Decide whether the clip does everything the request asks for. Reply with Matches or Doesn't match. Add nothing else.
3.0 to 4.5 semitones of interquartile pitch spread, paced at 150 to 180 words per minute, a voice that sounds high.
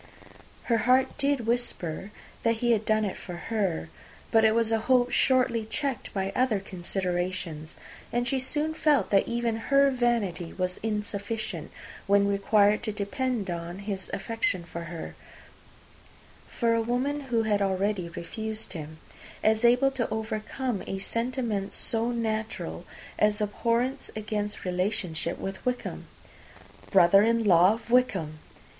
Doesn't match